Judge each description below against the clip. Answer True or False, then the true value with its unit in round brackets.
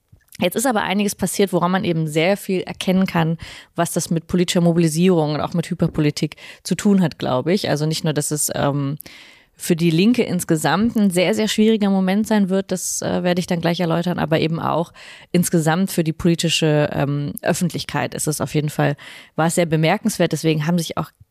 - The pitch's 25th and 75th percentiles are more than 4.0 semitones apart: False (2.8 semitones)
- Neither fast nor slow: False (205 wpm)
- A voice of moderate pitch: True (170 Hz)